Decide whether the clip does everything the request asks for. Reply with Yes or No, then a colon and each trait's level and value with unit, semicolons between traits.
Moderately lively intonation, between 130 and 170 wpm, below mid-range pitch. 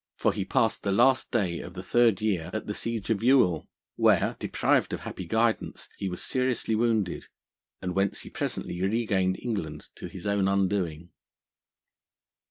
Yes: average, 3.6 semitones; average, 165 wpm; low, 100 Hz